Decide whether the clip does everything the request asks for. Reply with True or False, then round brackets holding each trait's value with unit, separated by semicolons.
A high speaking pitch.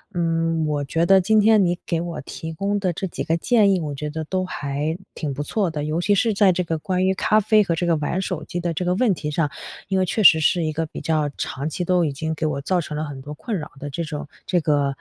False (165 Hz)